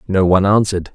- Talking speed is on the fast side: No, average, 190 wpm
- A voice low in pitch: Yes, very low, 95 Hz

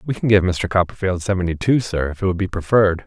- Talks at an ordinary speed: No, fast, 255 wpm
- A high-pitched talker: No, very low, 95 Hz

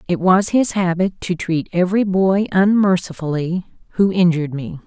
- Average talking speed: Yes, average, 150 wpm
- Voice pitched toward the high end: No, medium, 180 Hz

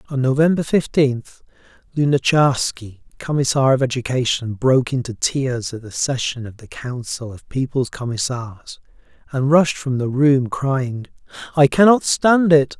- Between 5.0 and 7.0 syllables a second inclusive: No, 4.4 syllables/s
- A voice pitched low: Yes, low, 130 Hz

